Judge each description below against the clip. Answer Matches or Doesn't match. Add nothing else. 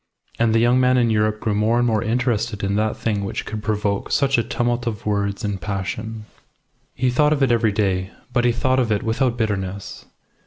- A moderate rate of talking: Doesn't match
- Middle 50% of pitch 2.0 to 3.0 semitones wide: Matches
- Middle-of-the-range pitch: Doesn't match